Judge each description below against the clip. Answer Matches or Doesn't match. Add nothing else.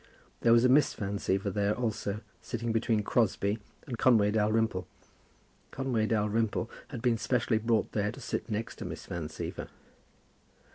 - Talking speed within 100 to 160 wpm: Matches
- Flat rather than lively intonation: Matches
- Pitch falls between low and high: Doesn't match